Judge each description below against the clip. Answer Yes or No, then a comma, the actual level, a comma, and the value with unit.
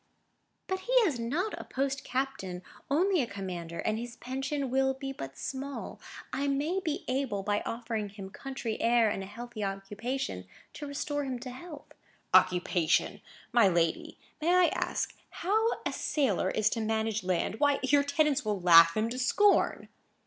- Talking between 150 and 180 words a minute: Yes, average, 165 wpm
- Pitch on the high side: Yes, very high, 250 Hz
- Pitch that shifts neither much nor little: No, wide, 5.8 semitones